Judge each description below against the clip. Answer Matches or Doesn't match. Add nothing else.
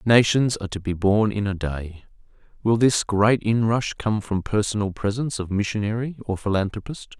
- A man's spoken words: Matches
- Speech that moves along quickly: Doesn't match